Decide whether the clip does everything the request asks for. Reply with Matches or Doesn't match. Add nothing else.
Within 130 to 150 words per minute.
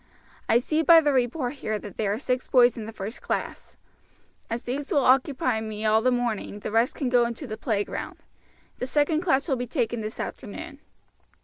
Doesn't match